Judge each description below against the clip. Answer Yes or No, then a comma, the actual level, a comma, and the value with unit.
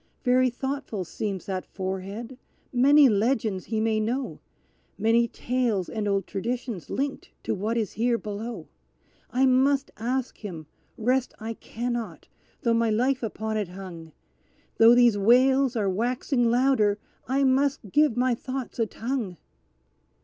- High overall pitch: Yes, high, 235 Hz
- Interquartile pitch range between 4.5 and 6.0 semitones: No, average, 3.4 semitones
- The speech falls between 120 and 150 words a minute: Yes, average, 140 wpm